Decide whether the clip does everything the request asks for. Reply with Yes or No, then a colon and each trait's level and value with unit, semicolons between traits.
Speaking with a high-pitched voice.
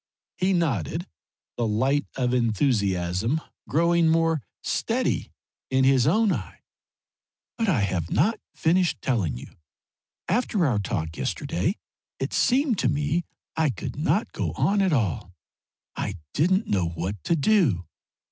No: medium, 140 Hz